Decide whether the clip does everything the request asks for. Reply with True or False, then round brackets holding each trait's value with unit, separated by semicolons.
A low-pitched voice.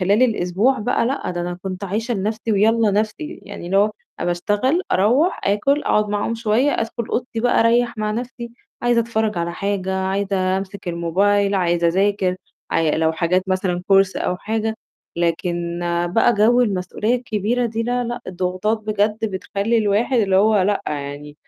False (205 Hz)